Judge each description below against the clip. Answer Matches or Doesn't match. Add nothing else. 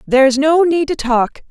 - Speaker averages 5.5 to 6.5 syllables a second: Doesn't match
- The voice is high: Matches